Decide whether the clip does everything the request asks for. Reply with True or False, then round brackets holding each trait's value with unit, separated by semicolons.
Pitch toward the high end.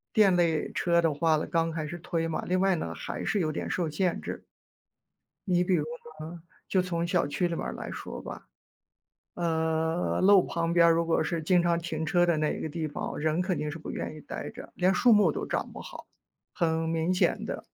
False (170 Hz)